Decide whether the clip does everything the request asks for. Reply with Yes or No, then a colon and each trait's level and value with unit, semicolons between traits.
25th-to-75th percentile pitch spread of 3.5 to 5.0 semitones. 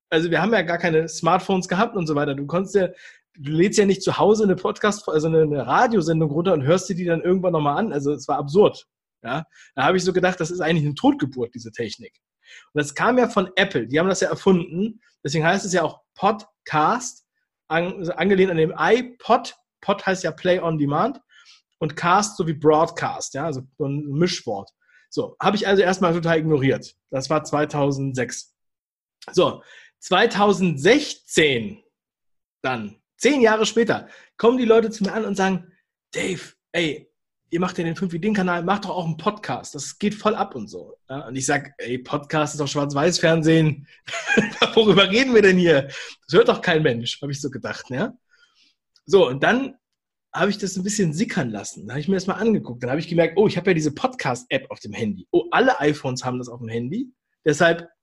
No: wide, 5.4 semitones